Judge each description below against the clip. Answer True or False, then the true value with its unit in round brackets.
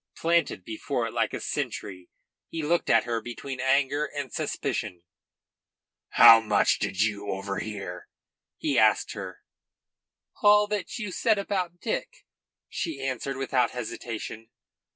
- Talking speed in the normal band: False (130 wpm)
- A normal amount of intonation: False (7.8 semitones)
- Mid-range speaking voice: False (130 Hz)